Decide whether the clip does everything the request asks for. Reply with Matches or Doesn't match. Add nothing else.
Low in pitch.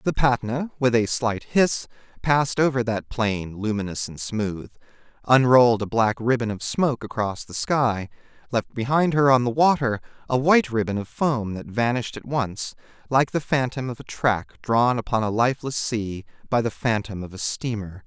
Matches